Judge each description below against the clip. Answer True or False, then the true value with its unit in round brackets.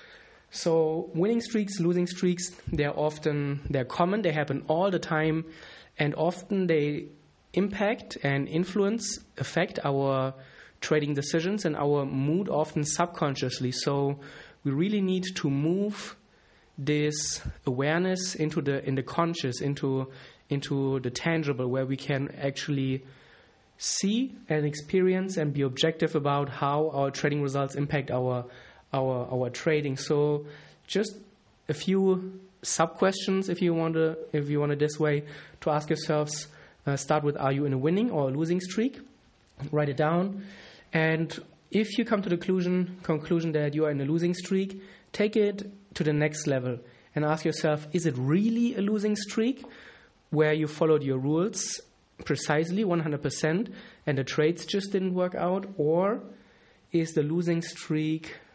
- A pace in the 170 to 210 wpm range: False (155 wpm)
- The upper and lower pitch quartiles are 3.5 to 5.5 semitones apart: True (4.3 semitones)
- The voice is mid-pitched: True (155 Hz)